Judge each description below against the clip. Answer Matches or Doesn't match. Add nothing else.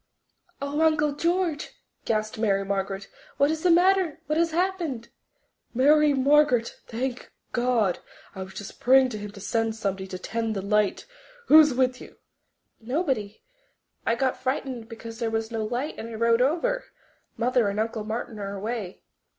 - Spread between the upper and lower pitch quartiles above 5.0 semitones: Matches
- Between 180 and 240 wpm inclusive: Doesn't match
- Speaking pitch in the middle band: Doesn't match